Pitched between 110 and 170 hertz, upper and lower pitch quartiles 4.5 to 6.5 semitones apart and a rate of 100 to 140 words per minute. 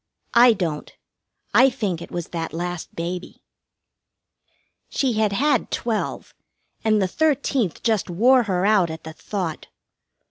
No: high, 200 Hz; wide, 5.4 semitones; slow, 135 wpm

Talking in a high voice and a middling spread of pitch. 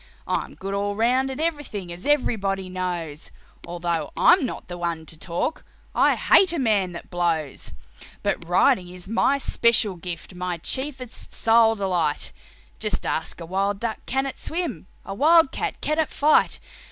No: high, 195 Hz; wide, 7.0 semitones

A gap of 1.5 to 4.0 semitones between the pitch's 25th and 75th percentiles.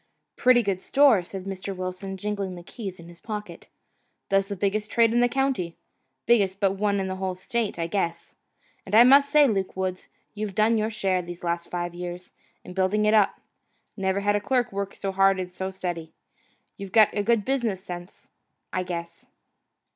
Yes: average, 2.7 semitones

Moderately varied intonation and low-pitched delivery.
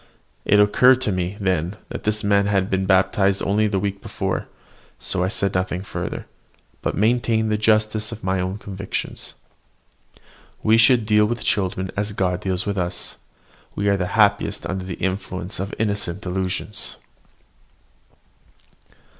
No: narrow, 2.2 semitones; low, 100 Hz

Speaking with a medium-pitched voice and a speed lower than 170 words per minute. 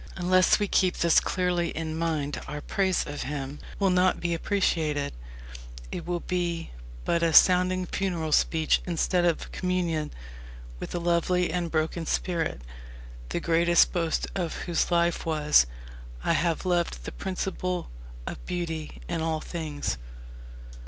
Yes: medium, 170 Hz; average, 140 wpm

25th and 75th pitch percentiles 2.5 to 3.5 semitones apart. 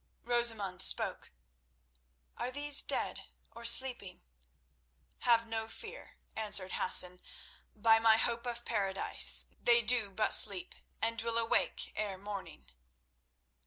Yes: average, 2.8 semitones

